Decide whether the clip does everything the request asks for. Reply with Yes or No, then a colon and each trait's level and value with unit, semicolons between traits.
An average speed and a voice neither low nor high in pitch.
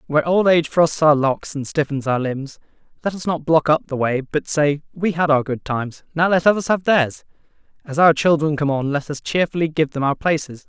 No: fast, 230 wpm; medium, 155 Hz